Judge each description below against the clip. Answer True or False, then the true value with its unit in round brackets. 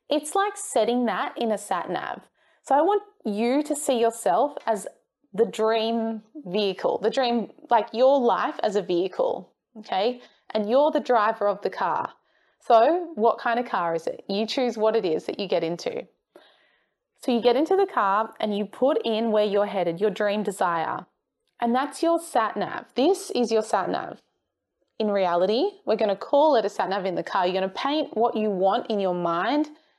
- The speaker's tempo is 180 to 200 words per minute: True (195 wpm)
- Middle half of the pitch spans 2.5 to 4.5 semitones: False (5.2 semitones)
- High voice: True (230 Hz)